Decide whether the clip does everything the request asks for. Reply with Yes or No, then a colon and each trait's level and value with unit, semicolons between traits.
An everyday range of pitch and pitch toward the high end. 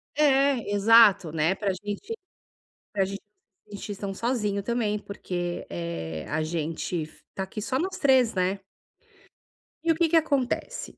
No: wide, 6.5 semitones; high, 205 Hz